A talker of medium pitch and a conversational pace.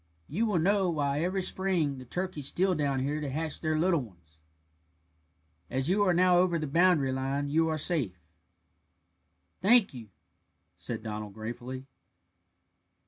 Yes: medium, 155 Hz; average, 150 wpm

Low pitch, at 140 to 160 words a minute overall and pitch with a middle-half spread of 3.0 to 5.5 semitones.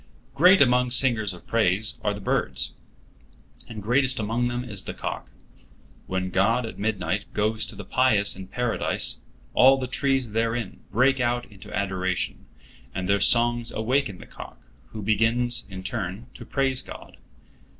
Yes: low, 115 Hz; average, 155 wpm; average, 3.7 semitones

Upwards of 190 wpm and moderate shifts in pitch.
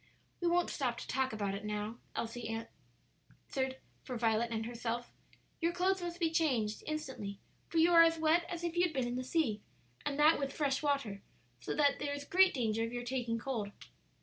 No: fast, 205 wpm; wide, 6.0 semitones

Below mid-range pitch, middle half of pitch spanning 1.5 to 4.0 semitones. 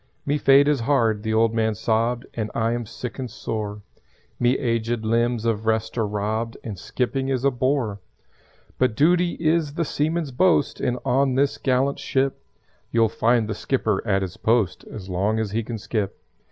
Yes: low, 115 Hz; average, 3.5 semitones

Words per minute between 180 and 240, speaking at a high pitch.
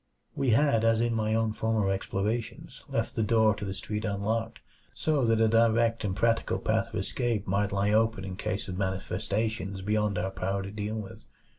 No: average, 190 wpm; low, 110 Hz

